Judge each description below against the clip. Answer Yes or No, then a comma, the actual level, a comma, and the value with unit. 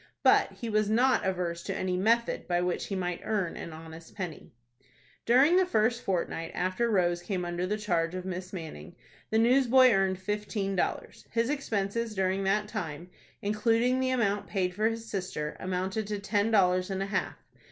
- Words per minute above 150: Yes, average, 180 wpm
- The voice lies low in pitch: No, high, 195 Hz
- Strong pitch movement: No, average, 3.7 semitones